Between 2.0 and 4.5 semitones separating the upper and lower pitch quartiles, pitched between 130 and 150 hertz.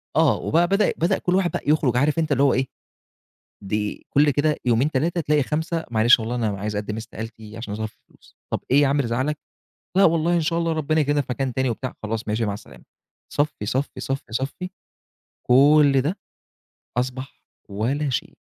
No: average, 5.0 semitones; low, 135 Hz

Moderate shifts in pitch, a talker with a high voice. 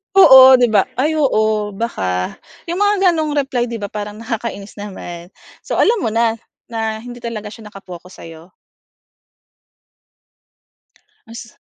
Yes: average, 4.1 semitones; high, 225 Hz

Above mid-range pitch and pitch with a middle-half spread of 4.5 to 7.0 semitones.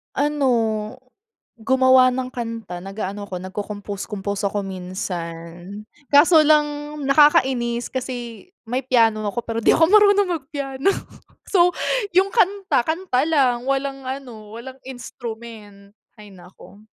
Yes: high, 245 Hz; average, 5.1 semitones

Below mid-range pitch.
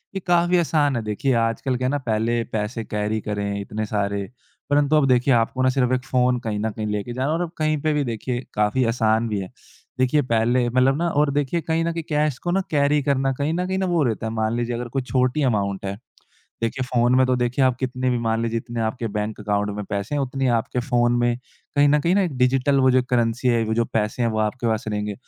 Yes: low, 125 Hz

